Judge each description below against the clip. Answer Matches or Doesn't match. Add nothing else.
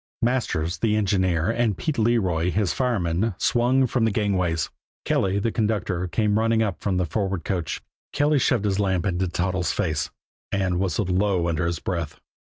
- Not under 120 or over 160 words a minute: Doesn't match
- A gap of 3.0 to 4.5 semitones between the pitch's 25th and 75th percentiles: Matches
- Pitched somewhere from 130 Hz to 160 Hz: Doesn't match